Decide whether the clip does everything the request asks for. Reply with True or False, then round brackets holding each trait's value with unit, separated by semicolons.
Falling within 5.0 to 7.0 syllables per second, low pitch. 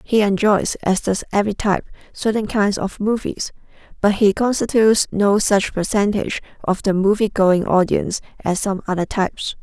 False (5.2 syllables/s; 200 Hz)